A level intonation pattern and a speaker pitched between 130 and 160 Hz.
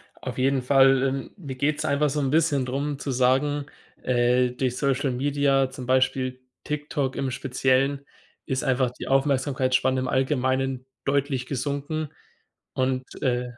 Yes: narrow, 1.6 semitones; low, 135 Hz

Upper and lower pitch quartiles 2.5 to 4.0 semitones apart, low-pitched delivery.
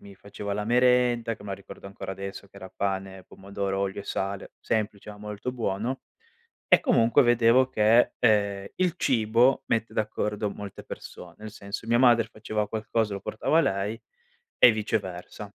Yes: average, 2.8 semitones; low, 105 Hz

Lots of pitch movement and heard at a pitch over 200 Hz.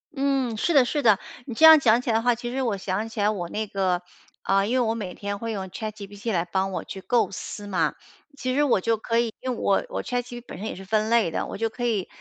No: average, 3.6 semitones; high, 220 Hz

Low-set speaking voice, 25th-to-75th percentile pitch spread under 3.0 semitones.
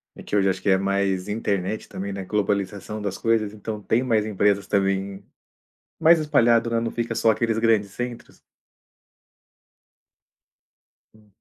Yes: low, 105 Hz; narrow, 2.5 semitones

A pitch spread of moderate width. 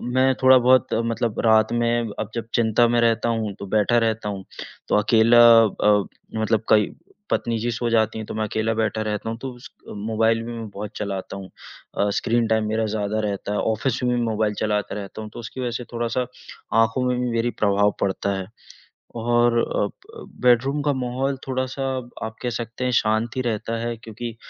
No: narrow, 1.9 semitones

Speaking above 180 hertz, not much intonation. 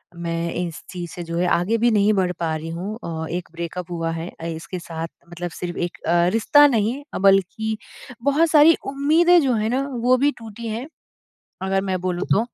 No: high, 190 Hz; wide, 5.4 semitones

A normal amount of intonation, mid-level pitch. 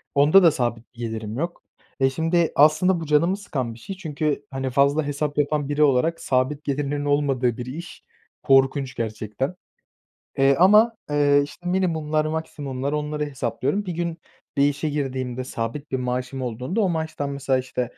Yes: average, 3.3 semitones; medium, 145 Hz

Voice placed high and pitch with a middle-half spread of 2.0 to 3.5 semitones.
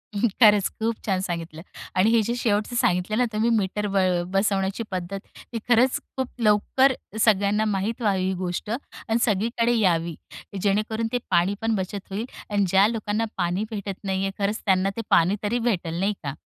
Yes: high, 205 Hz; average, 2.9 semitones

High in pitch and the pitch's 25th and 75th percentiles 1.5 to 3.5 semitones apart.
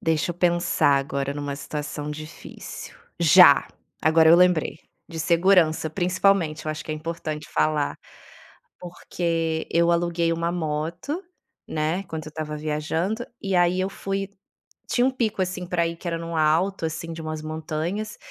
No: medium, 165 Hz; narrow, 2.4 semitones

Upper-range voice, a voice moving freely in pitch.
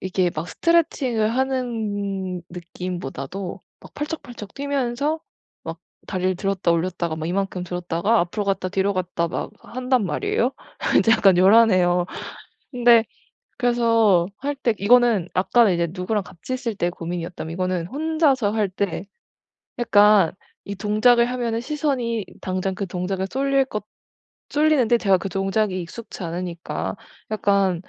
No: high, 200 Hz; average, 4.9 semitones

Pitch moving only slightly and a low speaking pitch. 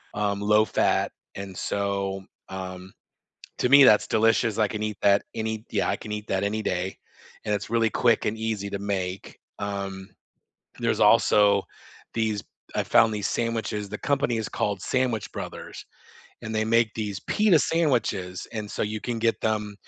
Yes: narrow, 2.0 semitones; low, 105 Hz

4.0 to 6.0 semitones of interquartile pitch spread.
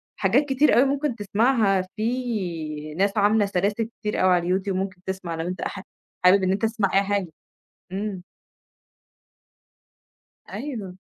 No: average, 3.1 semitones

